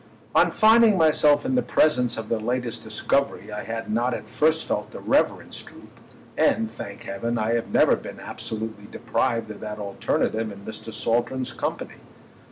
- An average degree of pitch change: Yes, average, 3.2 semitones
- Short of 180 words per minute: Yes, average, 160 wpm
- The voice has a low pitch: Yes, low, 115 Hz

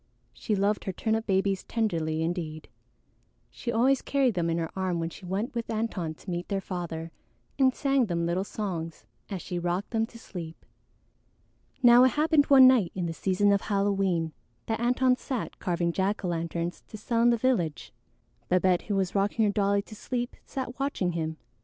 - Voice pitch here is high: Yes, high, 195 Hz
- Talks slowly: No, average, 185 wpm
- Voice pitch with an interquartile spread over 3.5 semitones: Yes, average, 5.1 semitones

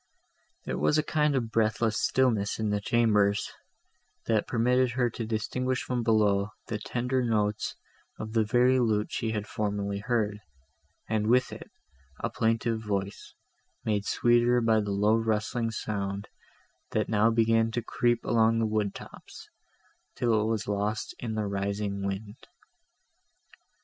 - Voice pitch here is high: No, low, 110 Hz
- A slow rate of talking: No, average, 145 wpm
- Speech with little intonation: Yes, narrow, 2.3 semitones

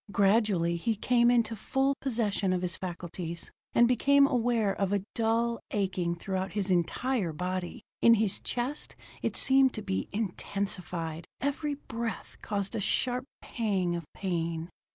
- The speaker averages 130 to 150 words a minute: Yes, average, 145 wpm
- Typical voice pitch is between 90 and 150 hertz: No, high, 205 Hz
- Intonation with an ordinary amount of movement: Yes, average, 4.8 semitones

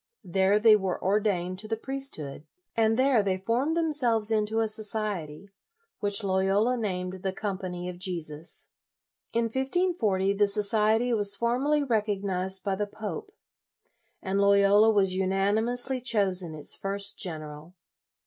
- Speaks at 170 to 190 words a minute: No, slow, 135 wpm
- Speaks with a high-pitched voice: Yes, high, 205 Hz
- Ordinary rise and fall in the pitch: Yes, average, 3.1 semitones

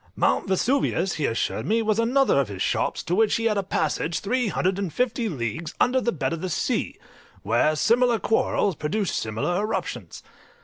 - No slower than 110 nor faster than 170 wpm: No, average, 185 wpm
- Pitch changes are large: Yes, wide, 6.4 semitones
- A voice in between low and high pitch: No, high, 195 Hz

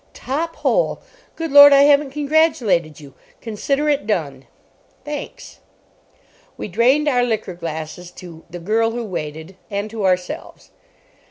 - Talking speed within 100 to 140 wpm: Yes, slow, 135 wpm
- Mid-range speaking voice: No, high, 220 Hz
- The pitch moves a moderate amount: No, wide, 8.5 semitones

